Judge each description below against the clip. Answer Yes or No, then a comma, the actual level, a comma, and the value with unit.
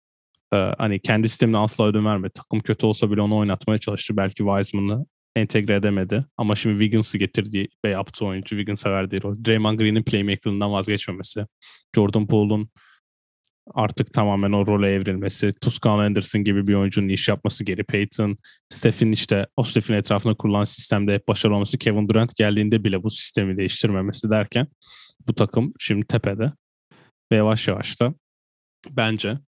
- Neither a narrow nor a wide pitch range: No, narrow, 1.8 semitones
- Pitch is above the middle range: No, low, 105 Hz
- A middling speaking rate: No, fast, 150 wpm